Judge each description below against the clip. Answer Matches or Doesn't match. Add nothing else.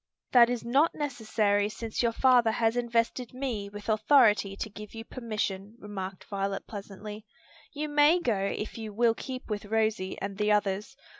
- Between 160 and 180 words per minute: Matches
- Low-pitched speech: Doesn't match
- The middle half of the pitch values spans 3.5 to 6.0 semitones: Doesn't match